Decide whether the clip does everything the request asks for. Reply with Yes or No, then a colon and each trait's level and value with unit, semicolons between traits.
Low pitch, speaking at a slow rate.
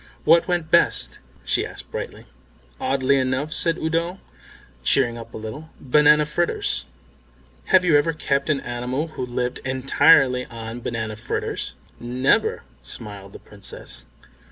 Yes: low, 130 Hz; slow, 130 wpm